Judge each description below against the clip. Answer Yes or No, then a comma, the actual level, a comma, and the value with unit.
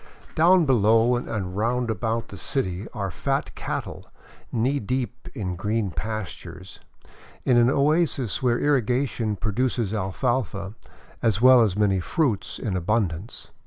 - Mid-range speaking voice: No, low, 115 Hz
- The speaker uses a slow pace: Yes, slow, 130 wpm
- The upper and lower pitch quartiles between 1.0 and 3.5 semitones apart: No, average, 4.2 semitones